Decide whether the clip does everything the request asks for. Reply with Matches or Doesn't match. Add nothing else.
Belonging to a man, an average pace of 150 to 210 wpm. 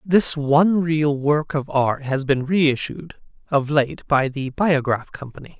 Matches